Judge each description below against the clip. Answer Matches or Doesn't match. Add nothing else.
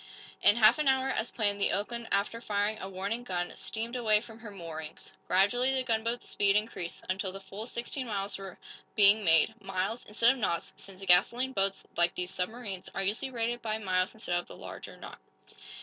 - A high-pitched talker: Matches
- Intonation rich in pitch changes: Doesn't match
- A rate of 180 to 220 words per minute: Matches